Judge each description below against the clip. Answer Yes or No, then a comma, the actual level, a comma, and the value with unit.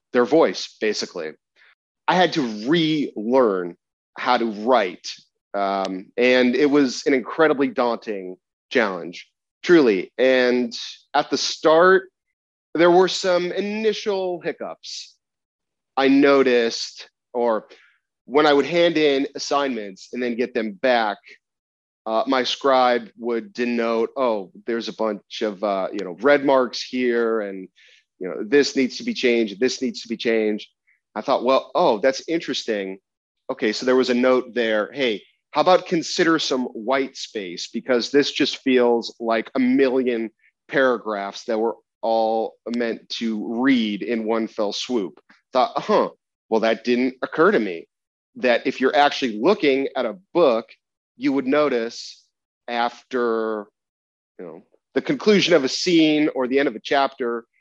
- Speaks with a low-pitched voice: Yes, low, 125 Hz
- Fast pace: No, average, 150 wpm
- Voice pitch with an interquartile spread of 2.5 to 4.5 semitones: Yes, average, 4.1 semitones